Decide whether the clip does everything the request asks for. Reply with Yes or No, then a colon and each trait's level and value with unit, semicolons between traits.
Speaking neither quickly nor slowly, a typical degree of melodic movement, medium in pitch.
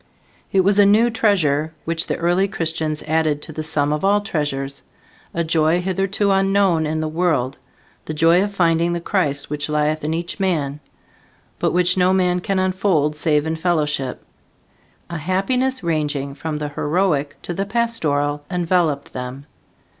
Yes: average, 160 wpm; average, 3.9 semitones; medium, 165 Hz